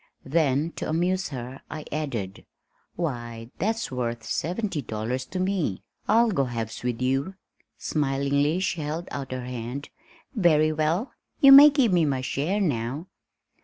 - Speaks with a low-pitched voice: No, medium, 145 Hz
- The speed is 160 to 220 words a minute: No, average, 150 wpm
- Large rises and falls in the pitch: Yes, wide, 6.0 semitones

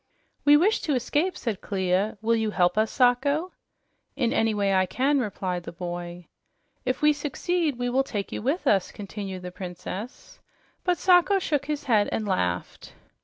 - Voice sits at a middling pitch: No, high, 225 Hz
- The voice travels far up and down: Yes, wide, 7.4 semitones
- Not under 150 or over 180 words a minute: Yes, average, 170 wpm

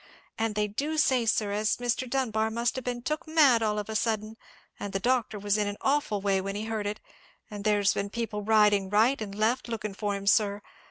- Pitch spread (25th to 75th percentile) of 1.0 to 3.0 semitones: Yes, narrow, 2.6 semitones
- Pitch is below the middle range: No, high, 215 Hz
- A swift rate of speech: Yes, fast, 225 wpm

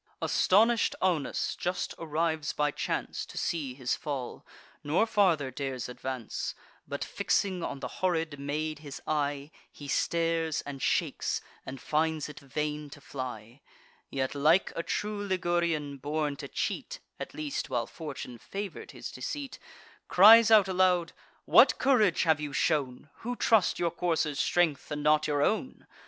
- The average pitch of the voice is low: No, medium, 155 Hz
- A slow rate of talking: No, average, 145 wpm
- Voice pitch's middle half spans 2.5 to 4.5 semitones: Yes, average, 4.2 semitones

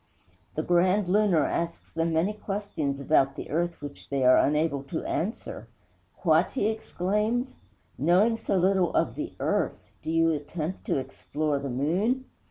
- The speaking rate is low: No, average, 155 wpm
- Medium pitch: Yes, medium, 170 Hz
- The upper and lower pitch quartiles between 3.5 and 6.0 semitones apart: Yes, average, 5.0 semitones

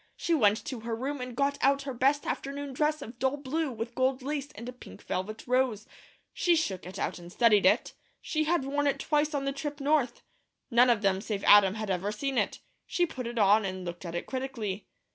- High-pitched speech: Yes, very high, 255 Hz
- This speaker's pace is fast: Yes, fast, 225 wpm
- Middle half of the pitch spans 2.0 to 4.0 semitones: No, average, 5.1 semitones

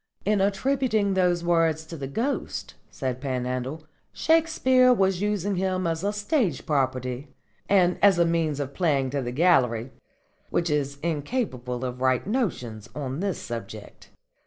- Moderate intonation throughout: No, wide, 7.2 semitones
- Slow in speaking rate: No, average, 145 wpm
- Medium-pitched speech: Yes, medium, 165 Hz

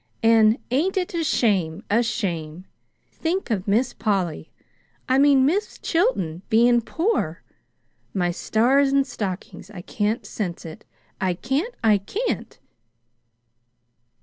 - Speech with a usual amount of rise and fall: No, wide, 6.6 semitones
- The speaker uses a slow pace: Yes, slow, 120 wpm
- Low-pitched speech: No, high, 225 Hz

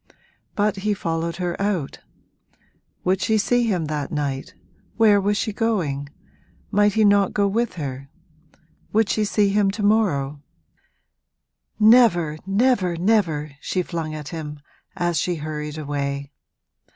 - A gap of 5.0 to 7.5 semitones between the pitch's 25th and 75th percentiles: Yes, wide, 5.5 semitones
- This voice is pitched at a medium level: Yes, medium, 180 Hz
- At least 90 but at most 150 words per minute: Yes, slow, 135 wpm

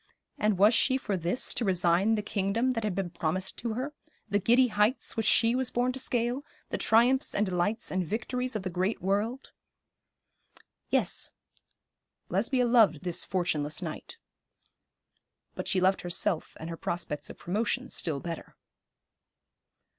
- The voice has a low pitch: No, high, 210 Hz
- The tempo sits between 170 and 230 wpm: No, average, 155 wpm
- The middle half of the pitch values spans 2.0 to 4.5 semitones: No, average, 5.0 semitones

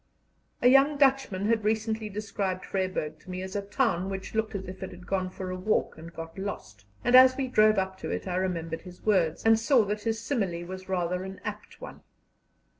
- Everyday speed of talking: No, fast, 215 wpm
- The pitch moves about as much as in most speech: Yes, average, 3.2 semitones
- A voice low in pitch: No, high, 195 Hz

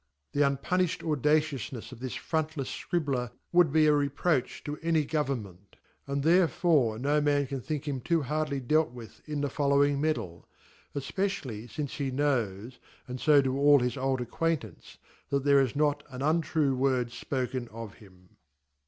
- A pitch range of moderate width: Yes, average, 3.2 semitones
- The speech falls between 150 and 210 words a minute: Yes, average, 160 wpm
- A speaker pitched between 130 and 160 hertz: Yes, medium, 140 Hz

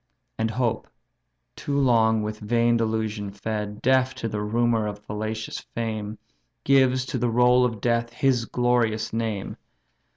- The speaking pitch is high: No, low, 115 Hz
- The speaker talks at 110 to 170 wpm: Yes, average, 140 wpm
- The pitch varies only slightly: Yes, narrow, 2.2 semitones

